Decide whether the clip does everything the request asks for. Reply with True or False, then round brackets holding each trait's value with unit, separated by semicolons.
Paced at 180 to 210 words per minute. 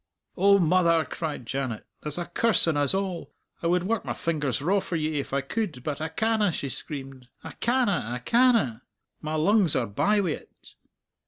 True (185 wpm)